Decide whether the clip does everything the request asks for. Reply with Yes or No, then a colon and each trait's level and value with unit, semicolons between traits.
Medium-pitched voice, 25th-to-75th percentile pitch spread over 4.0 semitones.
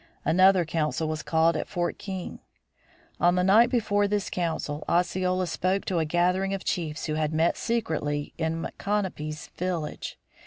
No: medium, 175 Hz; average, 3.2 semitones